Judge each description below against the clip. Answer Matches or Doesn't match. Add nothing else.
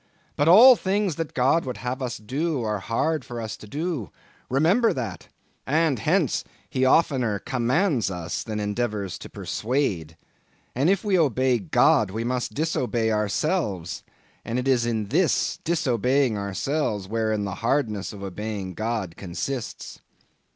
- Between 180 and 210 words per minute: Doesn't match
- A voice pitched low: Matches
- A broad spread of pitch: Matches